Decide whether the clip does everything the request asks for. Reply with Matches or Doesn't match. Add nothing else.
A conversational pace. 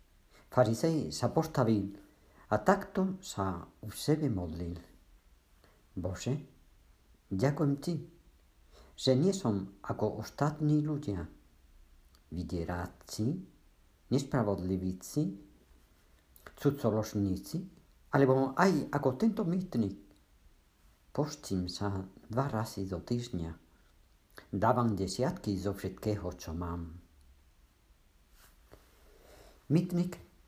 Doesn't match